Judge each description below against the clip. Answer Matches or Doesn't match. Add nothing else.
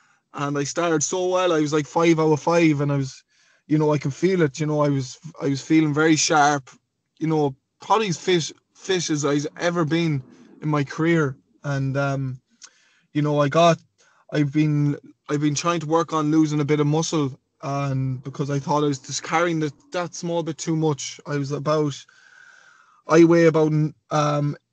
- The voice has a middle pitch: Matches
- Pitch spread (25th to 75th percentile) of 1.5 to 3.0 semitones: Matches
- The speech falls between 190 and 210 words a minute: Matches